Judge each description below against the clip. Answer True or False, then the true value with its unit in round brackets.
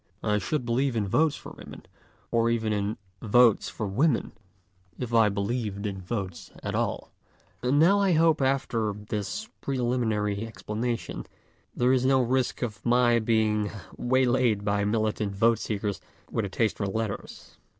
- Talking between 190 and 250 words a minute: False (150 wpm)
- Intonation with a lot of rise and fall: False (3.2 semitones)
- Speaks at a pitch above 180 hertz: False (115 Hz)